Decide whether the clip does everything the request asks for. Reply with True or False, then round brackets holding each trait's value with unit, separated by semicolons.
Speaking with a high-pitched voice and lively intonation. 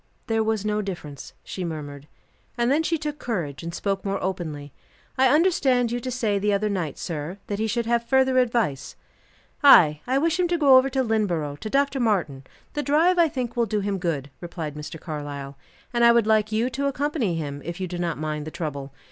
True (210 Hz; 8.2 semitones)